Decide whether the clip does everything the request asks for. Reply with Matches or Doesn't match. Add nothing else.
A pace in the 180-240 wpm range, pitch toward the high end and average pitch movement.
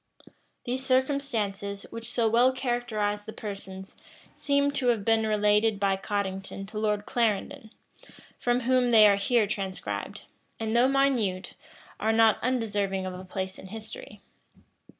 Doesn't match